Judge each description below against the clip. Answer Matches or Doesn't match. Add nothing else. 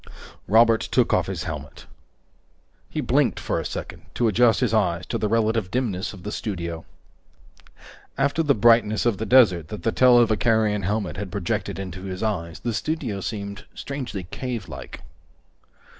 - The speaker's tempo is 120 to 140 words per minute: Doesn't match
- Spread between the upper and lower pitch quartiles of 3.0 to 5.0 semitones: Matches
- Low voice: Matches